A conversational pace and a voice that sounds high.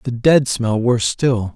No: average, 195 wpm; low, 120 Hz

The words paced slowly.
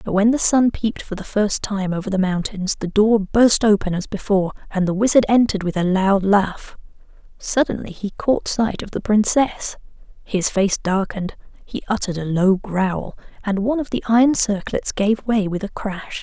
No: average, 190 wpm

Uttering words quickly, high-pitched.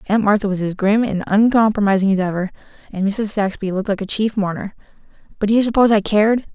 Yes: fast, 210 wpm; high, 205 Hz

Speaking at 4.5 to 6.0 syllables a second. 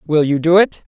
Yes: 5.6 syllables/s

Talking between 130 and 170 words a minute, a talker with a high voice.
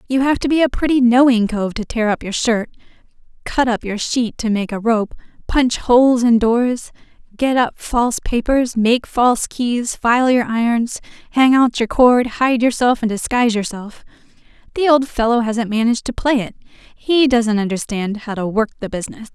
No: average, 185 wpm; high, 235 Hz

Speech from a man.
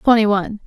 No: female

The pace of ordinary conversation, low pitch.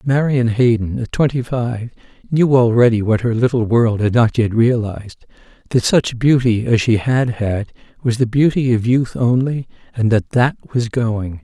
Yes: average, 175 wpm; low, 120 Hz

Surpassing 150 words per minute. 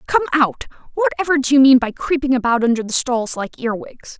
Yes: average, 200 wpm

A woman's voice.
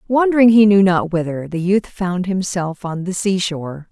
Yes: female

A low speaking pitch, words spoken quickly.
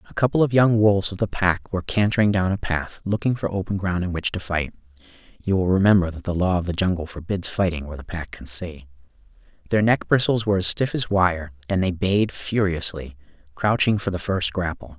Yes: very low, 95 Hz; fast, 215 wpm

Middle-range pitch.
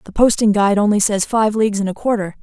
No: high, 210 Hz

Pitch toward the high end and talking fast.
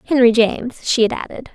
No: high, 240 Hz; average, 195 wpm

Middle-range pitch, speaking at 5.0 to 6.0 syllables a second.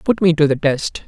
Yes: medium, 150 Hz; 5.2 syllables/s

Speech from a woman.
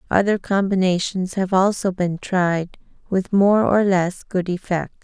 Yes: female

